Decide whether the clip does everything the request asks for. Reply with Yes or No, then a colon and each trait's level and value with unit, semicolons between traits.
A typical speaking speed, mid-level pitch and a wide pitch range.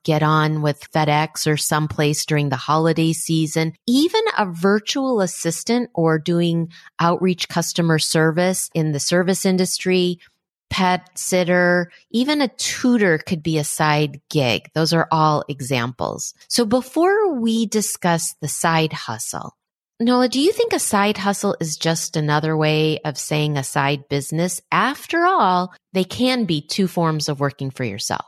No: average, 150 wpm; medium, 165 Hz; average, 4.3 semitones